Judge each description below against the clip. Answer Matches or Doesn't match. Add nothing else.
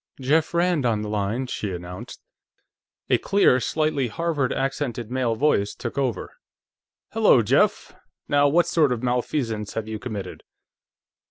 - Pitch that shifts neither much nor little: Matches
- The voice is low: Matches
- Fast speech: Doesn't match